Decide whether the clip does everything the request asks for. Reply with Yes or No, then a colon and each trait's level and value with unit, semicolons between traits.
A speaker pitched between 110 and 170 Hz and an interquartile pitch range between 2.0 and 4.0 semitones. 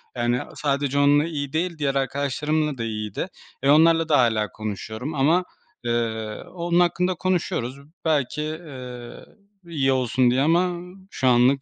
No: medium, 140 Hz; average, 4.6 semitones